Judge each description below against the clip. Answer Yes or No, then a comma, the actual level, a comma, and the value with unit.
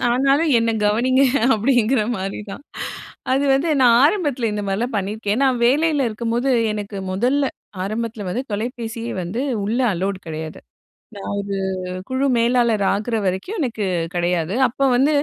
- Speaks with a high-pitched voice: Yes, high, 230 Hz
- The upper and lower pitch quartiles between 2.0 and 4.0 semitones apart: No, average, 4.4 semitones